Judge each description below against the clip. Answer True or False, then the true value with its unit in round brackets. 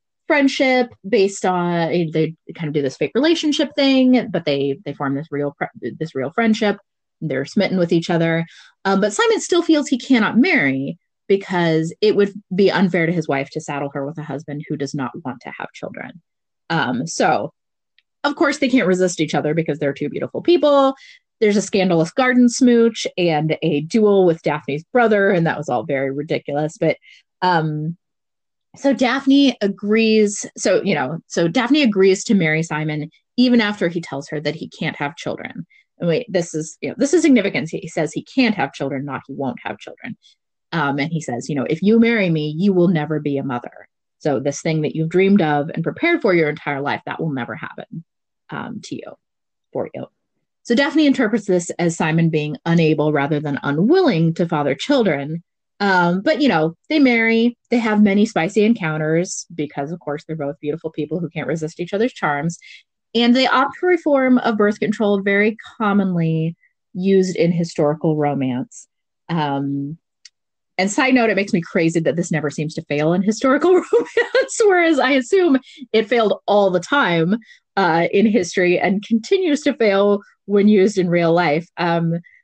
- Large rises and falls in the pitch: True (7.0 semitones)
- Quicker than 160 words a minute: True (190 wpm)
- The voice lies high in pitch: False (180 Hz)